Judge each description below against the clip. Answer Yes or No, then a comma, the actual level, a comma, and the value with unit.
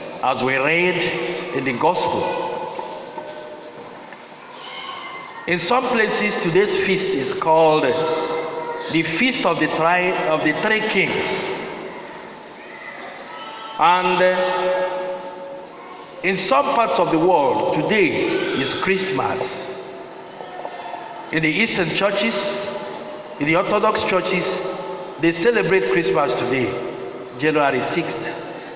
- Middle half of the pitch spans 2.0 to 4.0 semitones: No, average, 4.6 semitones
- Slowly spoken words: Yes, slow, 95 wpm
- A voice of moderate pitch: Yes, medium, 180 Hz